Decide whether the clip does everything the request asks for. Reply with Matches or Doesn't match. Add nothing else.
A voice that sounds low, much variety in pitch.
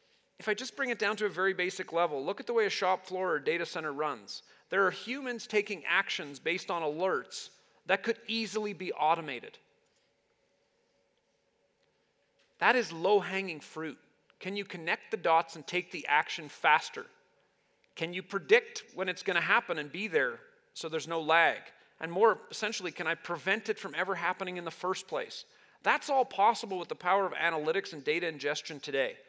Doesn't match